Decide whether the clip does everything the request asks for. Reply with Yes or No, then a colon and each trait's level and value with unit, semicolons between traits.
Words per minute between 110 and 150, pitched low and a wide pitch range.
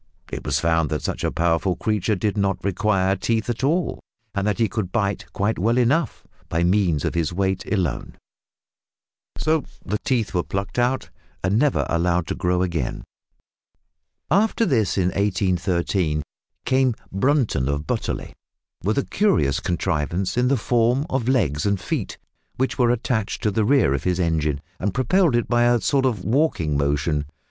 No: average, 165 wpm; low, 100 Hz; wide, 5.9 semitones